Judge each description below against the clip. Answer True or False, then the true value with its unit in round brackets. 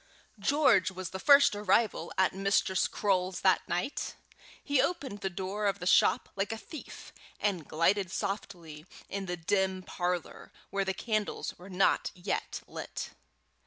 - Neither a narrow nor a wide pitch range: False (2.2 semitones)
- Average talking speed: True (150 wpm)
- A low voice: False (195 Hz)